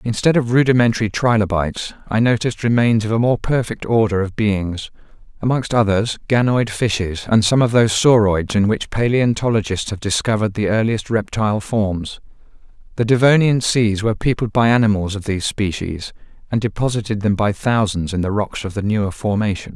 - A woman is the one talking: No, male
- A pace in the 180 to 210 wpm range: No, average, 165 wpm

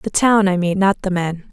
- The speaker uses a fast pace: Yes, fast, 275 wpm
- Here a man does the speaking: No, female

